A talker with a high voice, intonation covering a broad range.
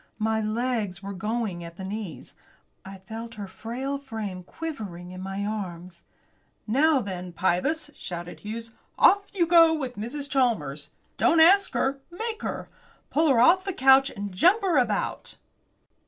Yes: high, 225 Hz; wide, 6.8 semitones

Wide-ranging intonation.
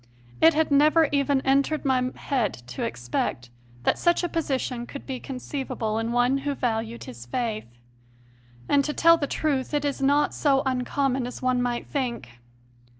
No: average, 3.1 semitones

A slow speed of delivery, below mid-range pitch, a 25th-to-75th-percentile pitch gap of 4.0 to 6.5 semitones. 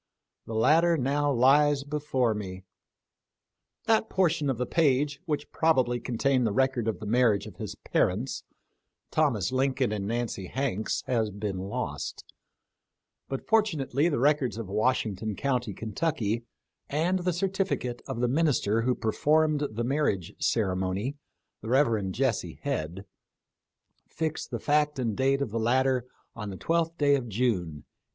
No: average, 150 wpm; low, 130 Hz; average, 5.1 semitones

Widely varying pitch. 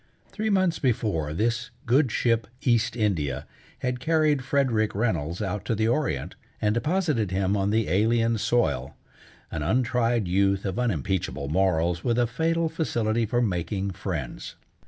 No: average, 4.6 semitones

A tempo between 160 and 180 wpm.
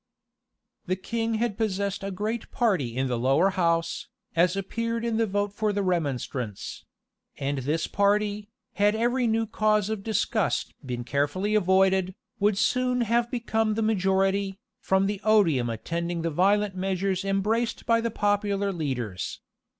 No: average, 150 wpm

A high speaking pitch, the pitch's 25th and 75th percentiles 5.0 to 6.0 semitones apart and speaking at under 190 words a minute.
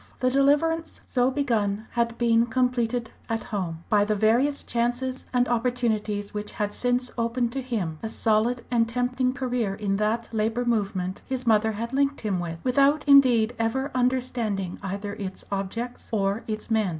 No: high, 230 Hz; average, 3.0 semitones; average, 160 wpm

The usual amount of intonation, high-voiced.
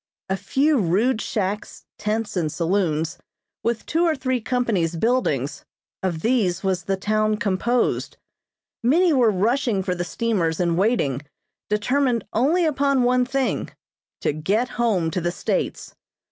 No: wide, 5.7 semitones; high, 215 Hz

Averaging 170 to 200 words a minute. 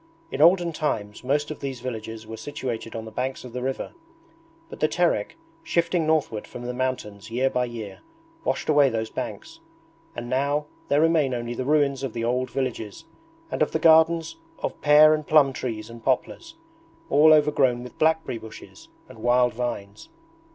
Yes: average, 175 wpm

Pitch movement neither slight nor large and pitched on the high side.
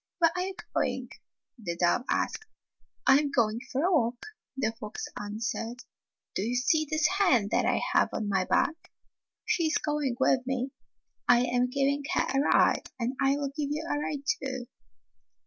Yes: average, 4.1 semitones; very high, 270 Hz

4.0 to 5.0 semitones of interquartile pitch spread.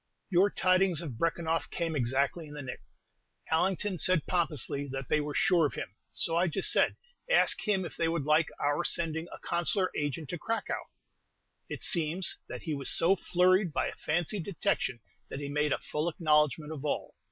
No: average, 3.2 semitones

